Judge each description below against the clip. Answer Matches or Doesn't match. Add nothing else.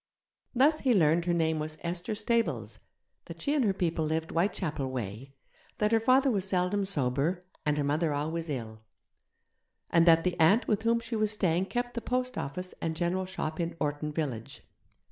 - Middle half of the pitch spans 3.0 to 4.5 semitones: Doesn't match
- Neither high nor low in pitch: Matches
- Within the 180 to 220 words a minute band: Matches